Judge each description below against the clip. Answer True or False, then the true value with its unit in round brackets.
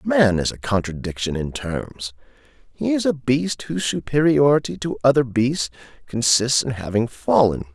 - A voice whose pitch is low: True (125 Hz)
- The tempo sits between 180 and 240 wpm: False (145 wpm)